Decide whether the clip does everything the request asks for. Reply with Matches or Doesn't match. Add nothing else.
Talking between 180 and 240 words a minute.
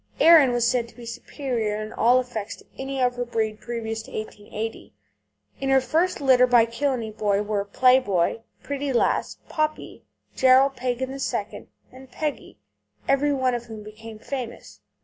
Doesn't match